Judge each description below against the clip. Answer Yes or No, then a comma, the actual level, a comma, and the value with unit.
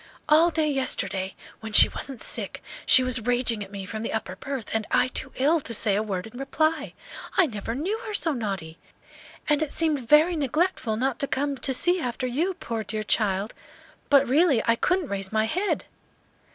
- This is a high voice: Yes, very high, 255 Hz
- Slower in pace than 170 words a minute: No, average, 195 wpm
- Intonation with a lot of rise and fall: Yes, wide, 5.8 semitones